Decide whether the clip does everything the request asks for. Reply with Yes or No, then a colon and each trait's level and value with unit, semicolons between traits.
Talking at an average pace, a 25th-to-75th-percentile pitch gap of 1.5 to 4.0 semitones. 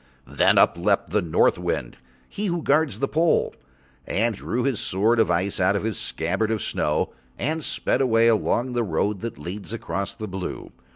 No: average, 185 wpm; average, 4.5 semitones